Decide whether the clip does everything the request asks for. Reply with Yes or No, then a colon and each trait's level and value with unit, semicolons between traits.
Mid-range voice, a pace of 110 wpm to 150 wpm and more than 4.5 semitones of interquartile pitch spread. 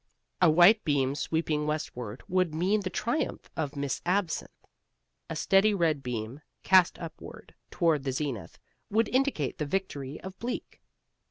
Yes: medium, 160 Hz; average, 145 wpm; average, 5.1 semitones